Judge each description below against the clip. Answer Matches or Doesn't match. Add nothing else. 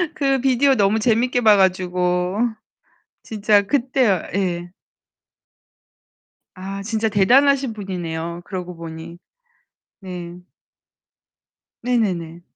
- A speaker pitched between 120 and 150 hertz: Doesn't match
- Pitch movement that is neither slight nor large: Matches